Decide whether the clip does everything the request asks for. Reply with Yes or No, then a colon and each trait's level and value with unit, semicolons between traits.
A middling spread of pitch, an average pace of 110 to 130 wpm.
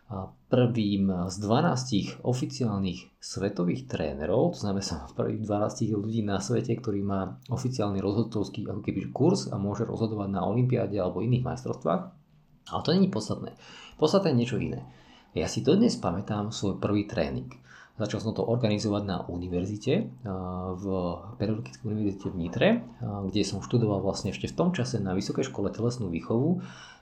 No: average, 3.2 semitones; average, 155 wpm